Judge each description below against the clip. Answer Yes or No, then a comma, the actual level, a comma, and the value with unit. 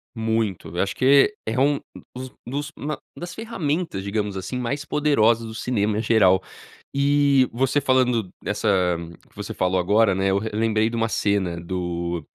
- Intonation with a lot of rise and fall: Yes, wide, 5.7 semitones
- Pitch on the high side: No, low, 115 Hz